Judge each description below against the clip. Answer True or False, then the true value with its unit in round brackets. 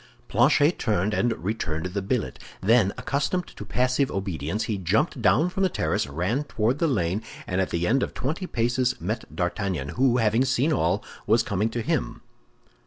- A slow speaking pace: False (175 wpm)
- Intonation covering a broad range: True (5.8 semitones)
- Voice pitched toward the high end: False (110 Hz)